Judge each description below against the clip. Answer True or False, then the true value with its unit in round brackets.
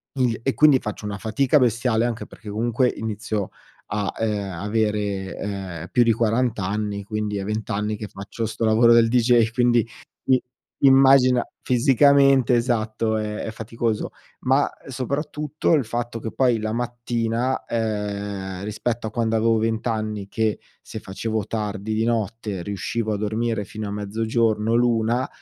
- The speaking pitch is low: True (110 Hz)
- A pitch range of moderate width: False (2.2 semitones)